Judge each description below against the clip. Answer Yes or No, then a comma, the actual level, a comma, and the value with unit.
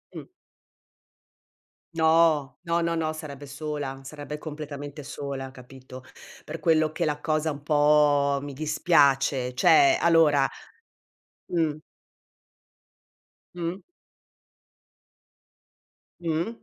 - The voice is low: No, medium, 150 Hz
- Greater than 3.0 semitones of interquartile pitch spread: No, narrow, 2.4 semitones